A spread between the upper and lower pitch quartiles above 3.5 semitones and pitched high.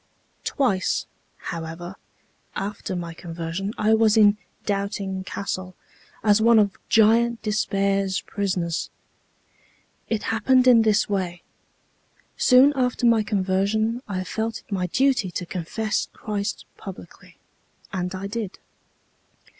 No: average, 2.9 semitones; high, 205 Hz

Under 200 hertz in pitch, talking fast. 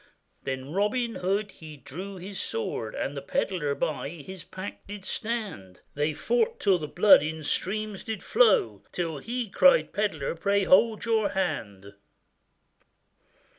No: medium, 185 Hz; average, 140 wpm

